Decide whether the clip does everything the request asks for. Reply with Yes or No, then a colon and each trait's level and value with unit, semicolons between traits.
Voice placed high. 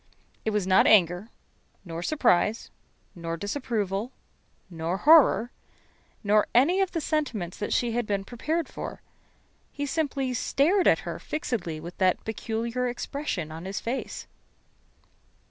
Yes: high, 225 Hz